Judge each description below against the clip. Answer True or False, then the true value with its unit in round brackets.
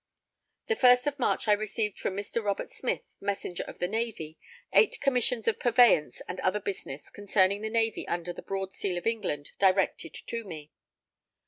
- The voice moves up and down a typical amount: True (3.7 semitones)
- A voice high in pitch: True (205 Hz)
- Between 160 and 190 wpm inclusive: True (175 wpm)